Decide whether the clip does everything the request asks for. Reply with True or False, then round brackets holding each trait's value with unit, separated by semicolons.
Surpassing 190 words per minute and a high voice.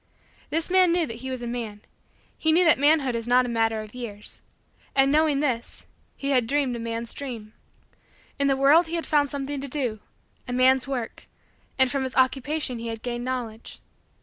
True (200 wpm; 260 Hz)